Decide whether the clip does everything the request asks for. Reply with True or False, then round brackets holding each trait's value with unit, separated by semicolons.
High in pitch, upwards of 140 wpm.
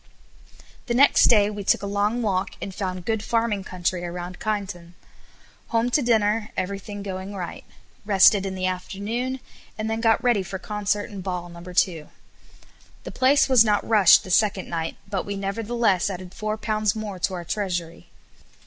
True (200 Hz; 170 wpm)